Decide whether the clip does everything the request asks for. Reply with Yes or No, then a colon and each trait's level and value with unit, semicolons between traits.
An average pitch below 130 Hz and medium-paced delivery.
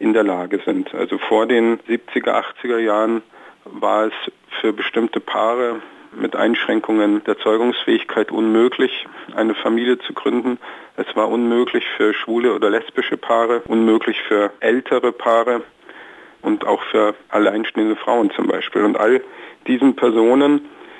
Yes: low, 115 Hz; average, 135 wpm